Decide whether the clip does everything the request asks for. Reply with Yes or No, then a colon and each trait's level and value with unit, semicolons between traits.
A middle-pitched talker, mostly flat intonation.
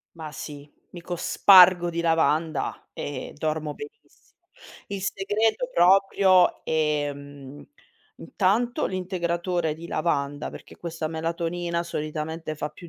No: medium, 170 Hz; average, 3.2 semitones